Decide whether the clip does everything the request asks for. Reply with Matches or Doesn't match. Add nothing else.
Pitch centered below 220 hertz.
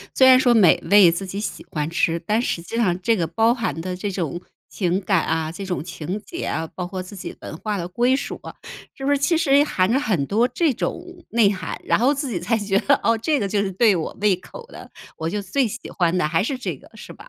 Matches